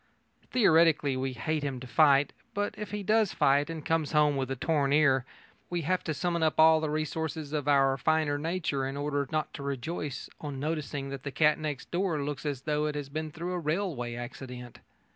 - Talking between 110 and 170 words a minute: No, fast, 205 wpm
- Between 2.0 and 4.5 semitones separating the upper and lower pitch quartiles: Yes, narrow, 2.6 semitones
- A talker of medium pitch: Yes, medium, 150 Hz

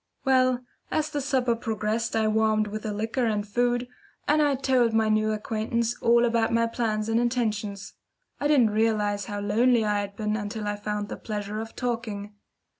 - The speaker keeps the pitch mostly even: Yes, narrow, 2.3 semitones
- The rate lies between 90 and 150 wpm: No, average, 190 wpm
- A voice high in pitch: Yes, high, 220 Hz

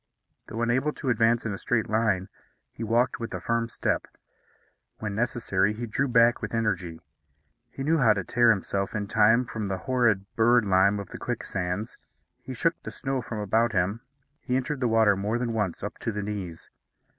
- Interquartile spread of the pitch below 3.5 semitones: Yes, average, 2.8 semitones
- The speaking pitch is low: Yes, low, 110 Hz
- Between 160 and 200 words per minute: Yes, average, 190 wpm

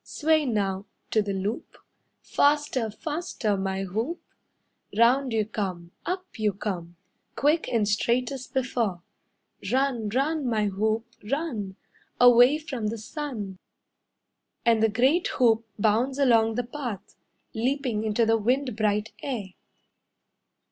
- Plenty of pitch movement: No, average, 4.2 semitones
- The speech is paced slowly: Yes, slow, 125 wpm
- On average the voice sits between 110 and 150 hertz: No, high, 230 Hz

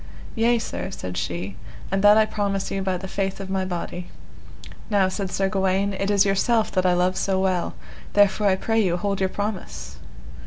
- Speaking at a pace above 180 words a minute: Yes, average, 195 wpm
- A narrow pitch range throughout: Yes, narrow, 1.6 semitones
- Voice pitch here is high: Yes, high, 195 Hz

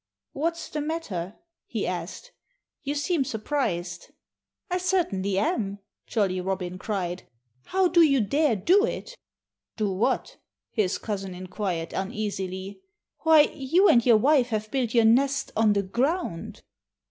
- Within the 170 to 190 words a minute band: No, slow, 135 wpm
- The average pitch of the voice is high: Yes, high, 220 Hz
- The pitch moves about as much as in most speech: No, wide, 7.5 semitones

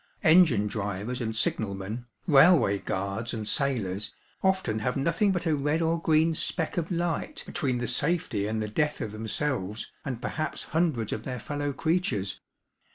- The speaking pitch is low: Yes, low, 130 Hz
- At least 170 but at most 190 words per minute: No, average, 160 wpm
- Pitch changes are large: Yes, wide, 7.1 semitones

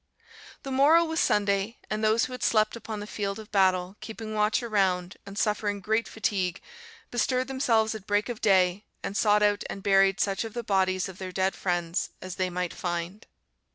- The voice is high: Yes, high, 205 Hz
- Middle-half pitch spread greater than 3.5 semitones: No, average, 2.7 semitones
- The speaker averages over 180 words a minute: Yes, average, 190 wpm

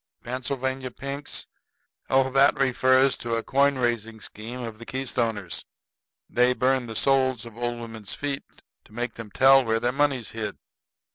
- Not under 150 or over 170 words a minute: Yes, average, 155 wpm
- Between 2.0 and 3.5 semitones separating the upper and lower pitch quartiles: Yes, narrow, 2.6 semitones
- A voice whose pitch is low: Yes, low, 125 Hz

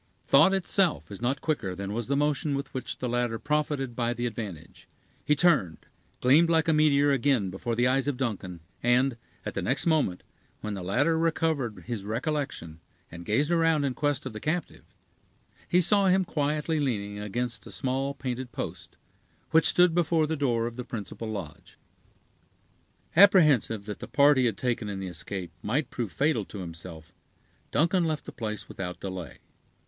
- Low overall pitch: Yes, low, 130 Hz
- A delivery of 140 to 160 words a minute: No, average, 175 wpm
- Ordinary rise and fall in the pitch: No, wide, 6.3 semitones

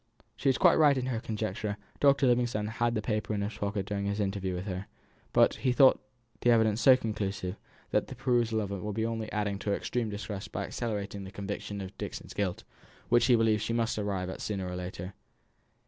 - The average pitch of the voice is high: No, low, 105 Hz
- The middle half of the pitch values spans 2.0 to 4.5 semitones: Yes, average, 2.7 semitones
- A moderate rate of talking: No, fast, 220 wpm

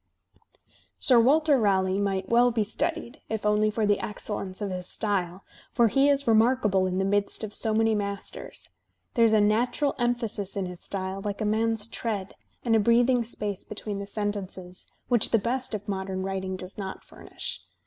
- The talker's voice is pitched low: No, high, 210 Hz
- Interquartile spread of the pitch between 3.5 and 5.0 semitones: No, average, 3.0 semitones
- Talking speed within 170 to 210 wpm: Yes, average, 180 wpm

